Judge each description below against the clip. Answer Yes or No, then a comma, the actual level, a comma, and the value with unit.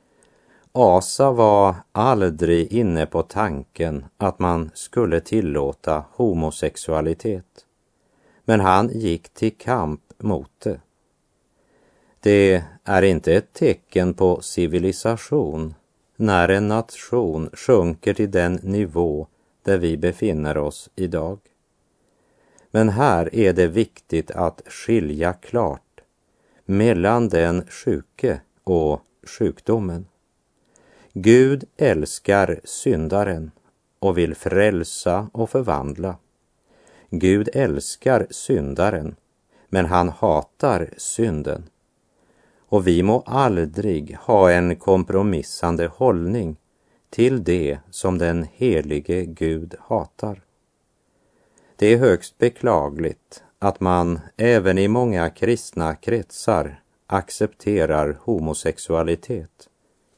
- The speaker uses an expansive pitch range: No, average, 4.3 semitones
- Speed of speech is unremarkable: No, slow, 95 wpm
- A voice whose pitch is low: Yes, very low, 90 Hz